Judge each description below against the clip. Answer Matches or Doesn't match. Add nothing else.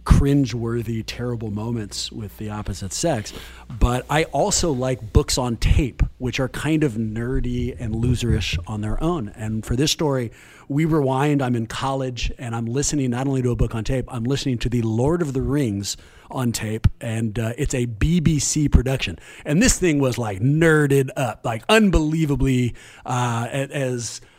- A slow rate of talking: Doesn't match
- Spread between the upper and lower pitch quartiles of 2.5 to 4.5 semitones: Matches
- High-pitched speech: Doesn't match